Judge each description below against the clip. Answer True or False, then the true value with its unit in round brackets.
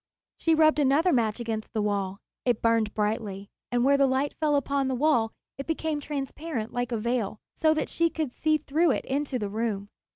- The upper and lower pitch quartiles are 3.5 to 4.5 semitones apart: False (5.2 semitones)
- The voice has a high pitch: True (260 Hz)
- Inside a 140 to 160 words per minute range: False (200 wpm)